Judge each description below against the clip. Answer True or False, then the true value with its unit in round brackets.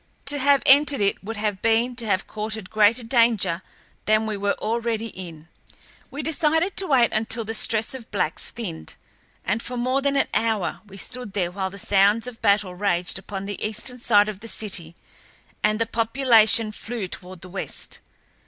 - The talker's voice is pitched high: True (220 Hz)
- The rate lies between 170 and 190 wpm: True (180 wpm)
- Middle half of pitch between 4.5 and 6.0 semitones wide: False (3.2 semitones)